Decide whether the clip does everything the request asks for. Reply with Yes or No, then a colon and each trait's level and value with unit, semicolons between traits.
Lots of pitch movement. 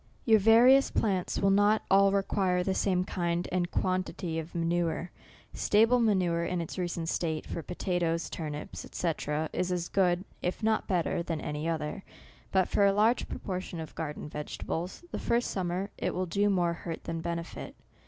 No: average, 2.8 semitones